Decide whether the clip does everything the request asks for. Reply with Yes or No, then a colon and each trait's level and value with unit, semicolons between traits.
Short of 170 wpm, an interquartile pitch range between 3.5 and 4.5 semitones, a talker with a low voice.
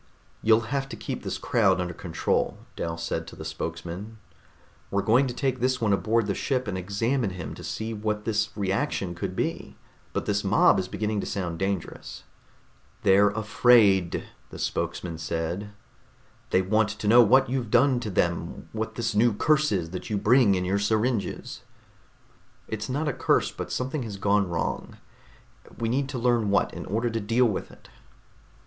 No: average, 180 wpm; average, 3.8 semitones; low, 105 Hz